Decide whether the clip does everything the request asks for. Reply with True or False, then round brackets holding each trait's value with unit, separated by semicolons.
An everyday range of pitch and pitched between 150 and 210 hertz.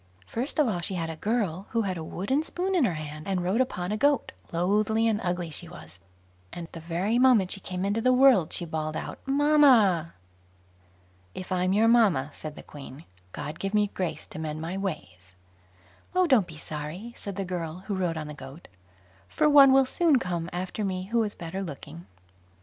False (5.7 semitones; 185 Hz)